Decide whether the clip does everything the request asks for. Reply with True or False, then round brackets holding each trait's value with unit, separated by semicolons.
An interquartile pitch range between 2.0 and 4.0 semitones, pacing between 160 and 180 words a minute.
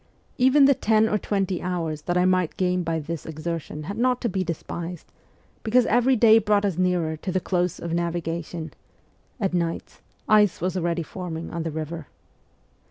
True (3.7 semitones; 175 wpm)